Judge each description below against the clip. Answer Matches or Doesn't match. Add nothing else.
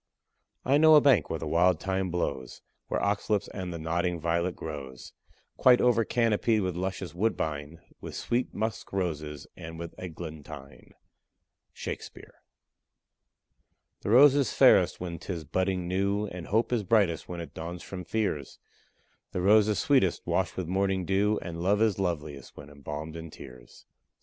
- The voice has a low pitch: Matches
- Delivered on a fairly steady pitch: Doesn't match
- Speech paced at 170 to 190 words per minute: Doesn't match